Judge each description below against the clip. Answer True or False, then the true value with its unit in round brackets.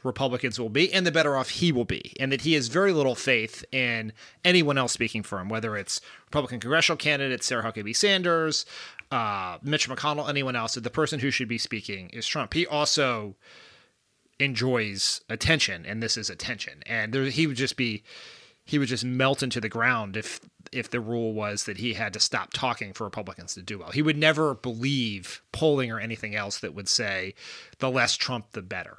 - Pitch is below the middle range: True (125 Hz)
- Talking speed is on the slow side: False (200 wpm)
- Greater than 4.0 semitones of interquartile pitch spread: True (4.4 semitones)